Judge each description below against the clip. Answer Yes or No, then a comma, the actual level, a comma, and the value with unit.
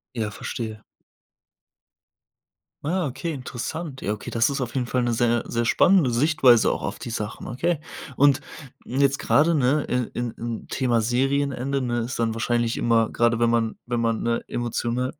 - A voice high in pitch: No, low, 120 Hz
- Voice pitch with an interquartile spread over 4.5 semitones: No, average, 2.8 semitones